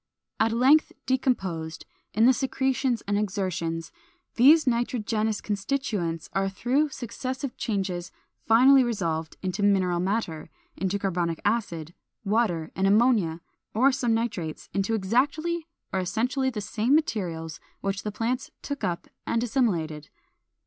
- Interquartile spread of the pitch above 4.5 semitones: Yes, wide, 5.5 semitones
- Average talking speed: No, slow, 125 wpm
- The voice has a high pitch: Yes, high, 215 Hz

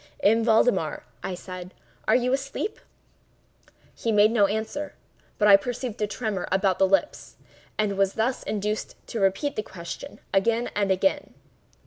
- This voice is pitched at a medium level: No, high, 210 Hz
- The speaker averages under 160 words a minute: Yes, average, 150 wpm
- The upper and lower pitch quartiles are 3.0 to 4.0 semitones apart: Yes, average, 3.3 semitones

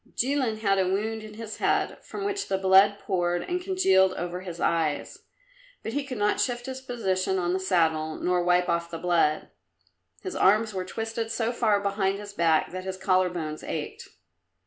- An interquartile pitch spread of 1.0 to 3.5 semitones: No, average, 4.0 semitones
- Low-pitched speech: No, high, 190 Hz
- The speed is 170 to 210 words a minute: Yes, average, 190 wpm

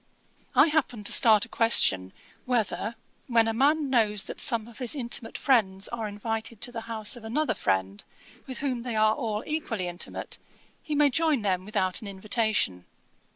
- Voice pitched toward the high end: Yes, high, 225 Hz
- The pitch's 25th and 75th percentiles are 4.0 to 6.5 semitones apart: No, average, 3.3 semitones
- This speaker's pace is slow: No, average, 175 wpm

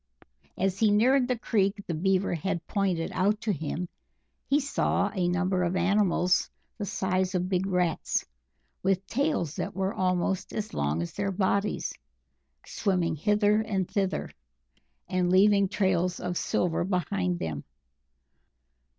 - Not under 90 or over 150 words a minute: Yes, average, 140 wpm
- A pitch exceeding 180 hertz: Yes, high, 190 Hz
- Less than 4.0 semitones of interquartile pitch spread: Yes, narrow, 2.4 semitones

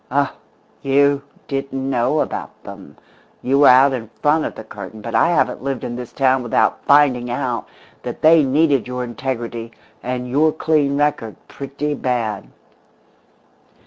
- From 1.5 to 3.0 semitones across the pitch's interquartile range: Yes, average, 2.7 semitones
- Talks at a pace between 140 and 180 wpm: Yes, average, 150 wpm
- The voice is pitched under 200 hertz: Yes, low, 135 Hz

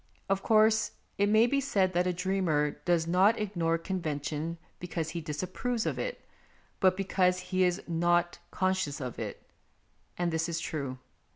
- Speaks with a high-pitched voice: No, medium, 180 Hz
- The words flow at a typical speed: Yes, average, 170 wpm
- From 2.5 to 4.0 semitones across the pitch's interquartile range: Yes, average, 2.9 semitones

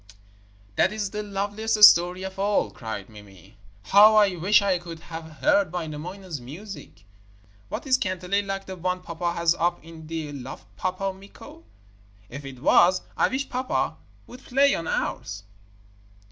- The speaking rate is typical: Yes, average, 155 wpm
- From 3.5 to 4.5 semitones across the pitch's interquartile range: Yes, average, 4.1 semitones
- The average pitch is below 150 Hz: No, medium, 180 Hz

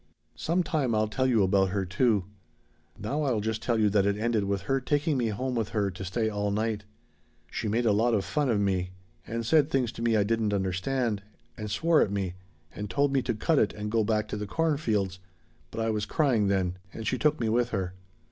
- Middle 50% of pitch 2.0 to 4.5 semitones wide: Yes, average, 3.7 semitones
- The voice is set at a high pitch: No, low, 110 Hz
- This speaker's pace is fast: Yes, fast, 230 wpm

